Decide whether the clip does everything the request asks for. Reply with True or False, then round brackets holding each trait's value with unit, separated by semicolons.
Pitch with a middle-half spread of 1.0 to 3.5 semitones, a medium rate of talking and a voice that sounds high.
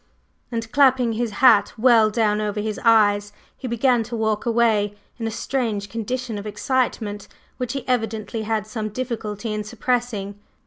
True (2.4 semitones; 160 wpm; 225 Hz)